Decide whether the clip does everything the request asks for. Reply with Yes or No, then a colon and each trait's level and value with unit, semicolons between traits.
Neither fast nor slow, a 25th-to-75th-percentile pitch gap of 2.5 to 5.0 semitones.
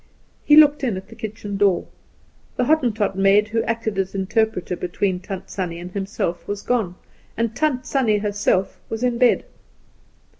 Yes: average, 160 wpm; average, 3.4 semitones